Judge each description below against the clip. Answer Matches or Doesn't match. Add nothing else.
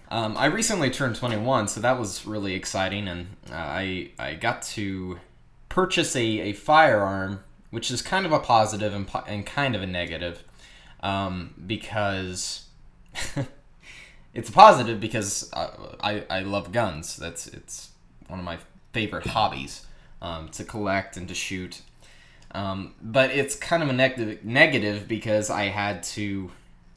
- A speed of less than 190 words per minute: Matches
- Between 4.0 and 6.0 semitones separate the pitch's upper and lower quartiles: Matches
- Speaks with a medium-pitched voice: Doesn't match